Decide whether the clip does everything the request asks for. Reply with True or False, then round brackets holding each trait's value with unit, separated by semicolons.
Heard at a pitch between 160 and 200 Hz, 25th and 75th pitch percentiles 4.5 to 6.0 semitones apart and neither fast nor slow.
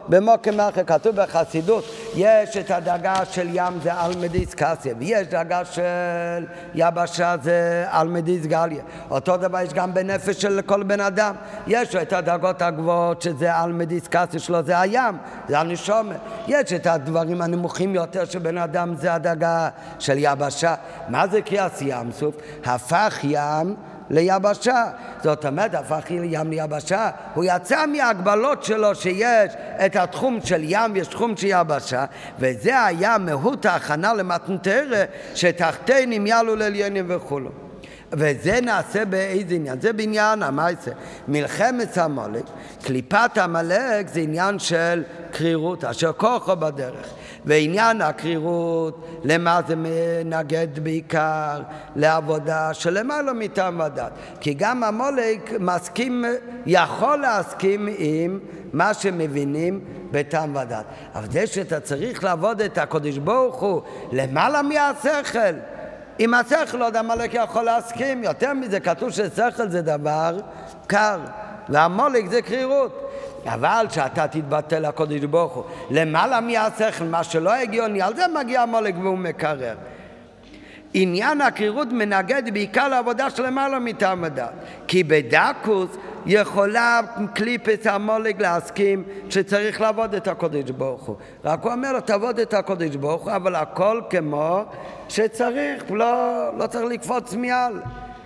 True (185 Hz; 5.2 semitones; 130 wpm)